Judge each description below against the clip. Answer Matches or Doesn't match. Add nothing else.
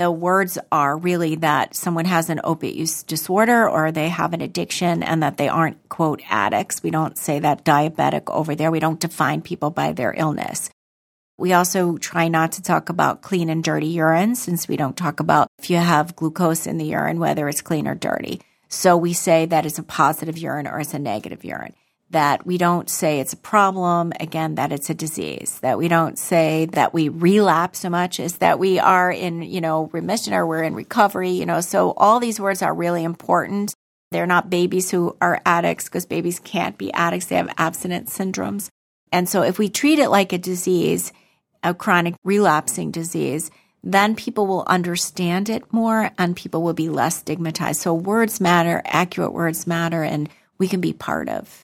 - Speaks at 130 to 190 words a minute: Doesn't match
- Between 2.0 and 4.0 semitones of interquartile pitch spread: Matches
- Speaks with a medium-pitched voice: Matches